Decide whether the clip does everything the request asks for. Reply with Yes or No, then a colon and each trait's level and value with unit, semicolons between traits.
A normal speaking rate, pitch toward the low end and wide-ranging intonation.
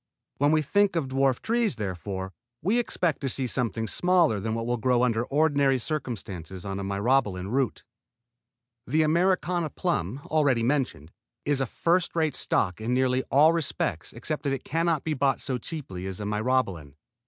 Yes: average, 175 wpm; low, 130 Hz; wide, 6.4 semitones